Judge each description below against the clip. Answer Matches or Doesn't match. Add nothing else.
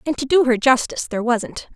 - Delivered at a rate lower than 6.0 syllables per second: Doesn't match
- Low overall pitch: Doesn't match